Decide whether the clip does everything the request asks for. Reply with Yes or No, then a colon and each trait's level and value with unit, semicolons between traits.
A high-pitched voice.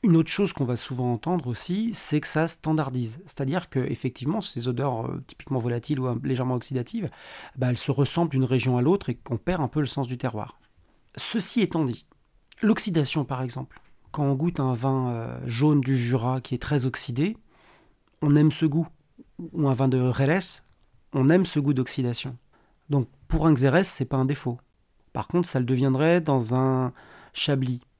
No: low, 135 Hz